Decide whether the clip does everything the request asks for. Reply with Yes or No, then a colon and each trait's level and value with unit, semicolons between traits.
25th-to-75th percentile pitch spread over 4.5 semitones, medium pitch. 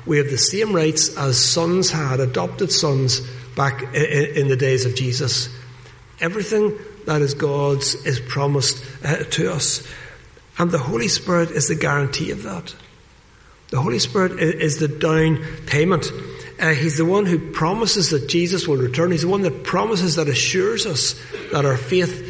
No: average, 4.0 semitones; medium, 150 Hz